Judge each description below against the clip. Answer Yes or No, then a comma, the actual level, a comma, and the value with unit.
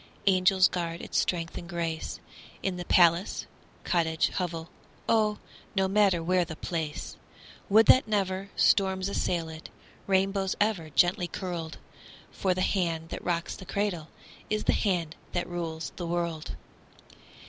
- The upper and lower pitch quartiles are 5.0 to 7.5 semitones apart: No, narrow, 2.5 semitones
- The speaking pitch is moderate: Yes, medium, 180 Hz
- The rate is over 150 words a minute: No, average, 140 wpm